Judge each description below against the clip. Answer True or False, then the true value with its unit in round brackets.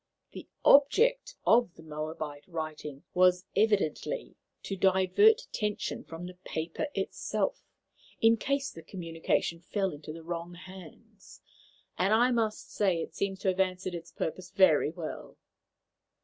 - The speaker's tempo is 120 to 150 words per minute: True (135 wpm)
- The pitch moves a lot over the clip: False (4.4 semitones)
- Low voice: False (185 Hz)